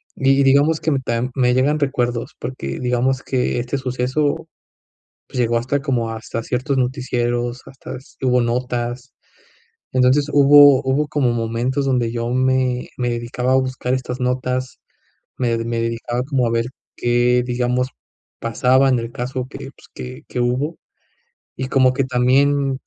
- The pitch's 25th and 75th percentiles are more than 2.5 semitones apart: No, narrow, 1.7 semitones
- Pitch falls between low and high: No, low, 125 Hz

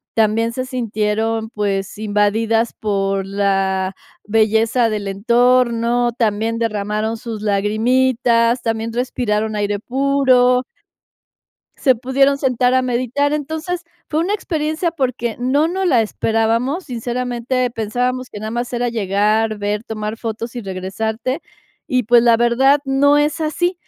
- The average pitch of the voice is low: No, high, 235 Hz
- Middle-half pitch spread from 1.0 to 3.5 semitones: Yes, average, 3.0 semitones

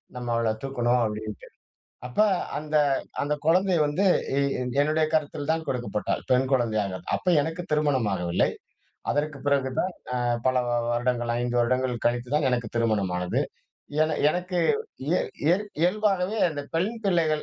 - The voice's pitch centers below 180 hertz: Yes, low, 135 Hz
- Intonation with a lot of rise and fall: No, average, 4.8 semitones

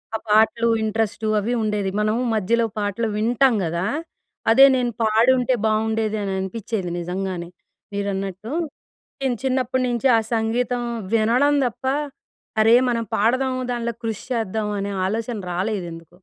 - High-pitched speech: Yes, high, 220 Hz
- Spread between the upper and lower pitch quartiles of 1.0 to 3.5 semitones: Yes, average, 2.8 semitones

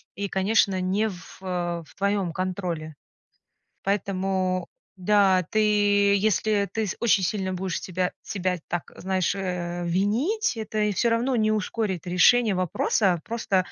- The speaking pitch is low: No, high, 190 Hz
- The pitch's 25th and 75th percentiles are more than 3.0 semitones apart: No, narrow, 2.6 semitones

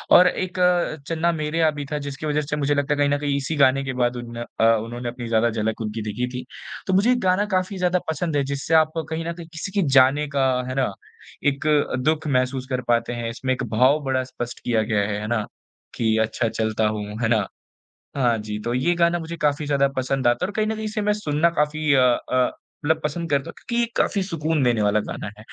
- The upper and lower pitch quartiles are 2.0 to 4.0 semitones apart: No, average, 5.1 semitones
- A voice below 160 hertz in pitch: Yes, medium, 140 Hz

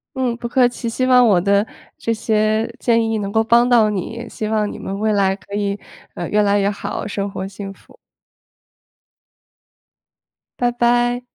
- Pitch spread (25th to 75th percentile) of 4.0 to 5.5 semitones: No, average, 2.9 semitones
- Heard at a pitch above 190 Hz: Yes, high, 215 Hz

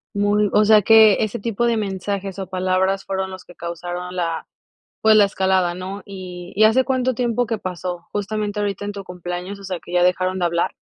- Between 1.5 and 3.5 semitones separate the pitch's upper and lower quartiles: Yes, narrow, 2.5 semitones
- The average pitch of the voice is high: Yes, high, 195 Hz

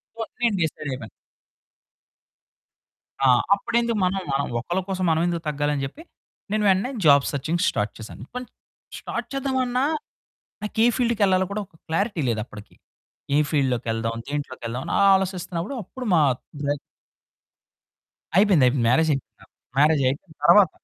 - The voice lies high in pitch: No, medium, 165 Hz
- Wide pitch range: Yes, wide, 6.9 semitones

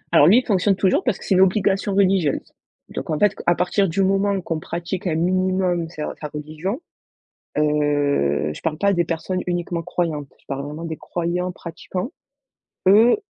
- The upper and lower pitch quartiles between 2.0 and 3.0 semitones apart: No, average, 3.5 semitones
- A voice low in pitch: No, medium, 175 Hz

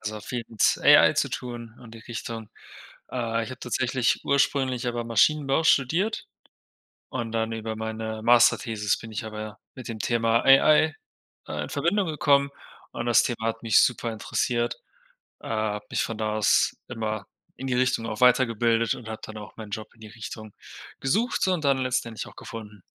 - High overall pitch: No, low, 115 Hz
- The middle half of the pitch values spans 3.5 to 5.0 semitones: No, average, 2.7 semitones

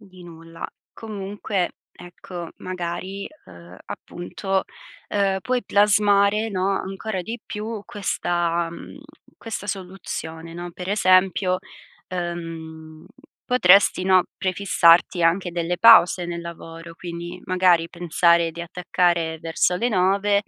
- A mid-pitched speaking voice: Yes, medium, 180 Hz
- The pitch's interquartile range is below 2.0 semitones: No, narrow, 2.6 semitones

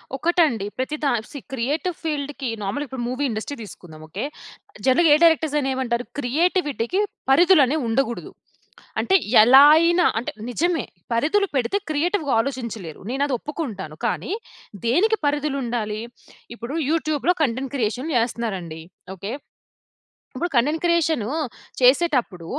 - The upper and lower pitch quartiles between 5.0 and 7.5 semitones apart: Yes, average, 5.3 semitones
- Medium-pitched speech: No, very high, 270 Hz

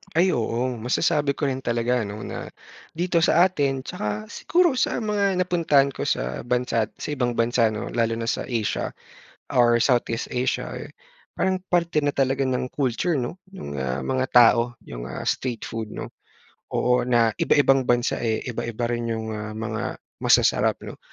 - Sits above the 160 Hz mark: No, low, 125 Hz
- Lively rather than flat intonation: No, average, 3.6 semitones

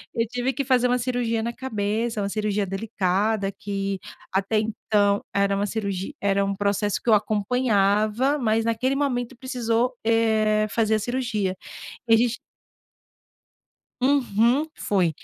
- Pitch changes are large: No, average, 3.3 semitones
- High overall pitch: Yes, high, 220 Hz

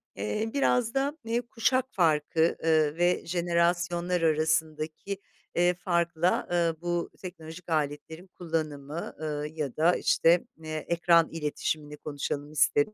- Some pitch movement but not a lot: No, narrow, 2.3 semitones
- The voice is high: No, medium, 165 Hz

